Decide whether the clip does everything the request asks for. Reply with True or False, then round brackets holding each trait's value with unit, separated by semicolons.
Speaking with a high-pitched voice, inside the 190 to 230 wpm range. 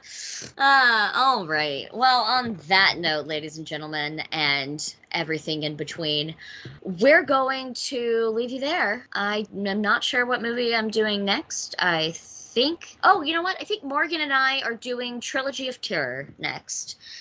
False (230 Hz; 160 wpm)